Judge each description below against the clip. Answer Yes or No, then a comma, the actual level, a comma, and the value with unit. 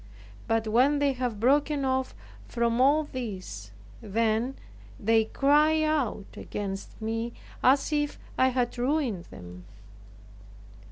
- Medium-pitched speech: No, high, 245 Hz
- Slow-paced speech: Yes, slow, 115 wpm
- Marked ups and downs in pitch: No, average, 4.2 semitones